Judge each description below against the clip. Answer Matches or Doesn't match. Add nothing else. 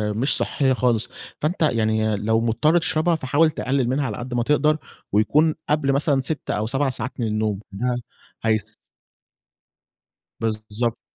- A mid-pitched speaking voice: Doesn't match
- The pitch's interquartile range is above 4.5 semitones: Matches